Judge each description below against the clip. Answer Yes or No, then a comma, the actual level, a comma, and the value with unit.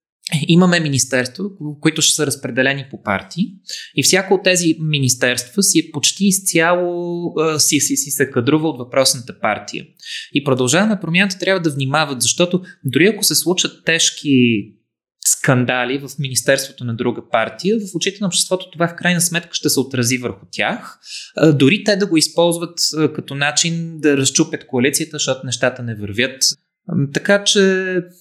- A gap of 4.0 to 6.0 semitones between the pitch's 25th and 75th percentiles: Yes, average, 4.8 semitones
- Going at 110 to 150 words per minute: No, average, 160 wpm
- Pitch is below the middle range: No, medium, 155 Hz